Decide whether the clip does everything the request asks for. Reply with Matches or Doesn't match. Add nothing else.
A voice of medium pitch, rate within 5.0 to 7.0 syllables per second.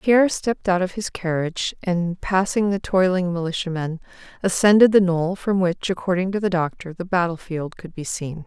Matches